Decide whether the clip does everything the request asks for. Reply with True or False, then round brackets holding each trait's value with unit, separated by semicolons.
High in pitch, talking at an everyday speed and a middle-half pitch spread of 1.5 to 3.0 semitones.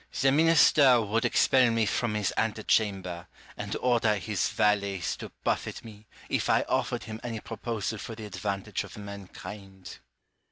False (105 Hz; 160 wpm; 2.4 semitones)